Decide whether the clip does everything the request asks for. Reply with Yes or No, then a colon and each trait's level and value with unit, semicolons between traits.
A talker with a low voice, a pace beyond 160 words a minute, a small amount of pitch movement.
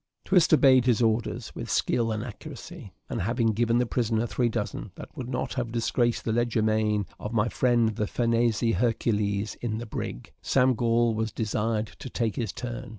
Yes: low, 115 Hz; average, 190 wpm; narrow, 1.8 semitones